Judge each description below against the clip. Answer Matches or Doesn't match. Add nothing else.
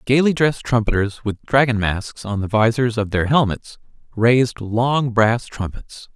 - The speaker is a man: Matches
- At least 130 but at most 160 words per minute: Matches